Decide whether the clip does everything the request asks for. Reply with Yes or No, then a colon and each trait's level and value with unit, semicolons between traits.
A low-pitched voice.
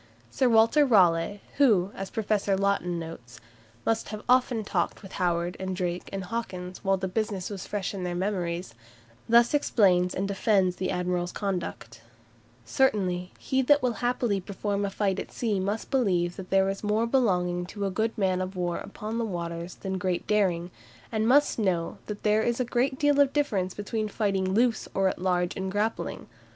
No: high, 195 Hz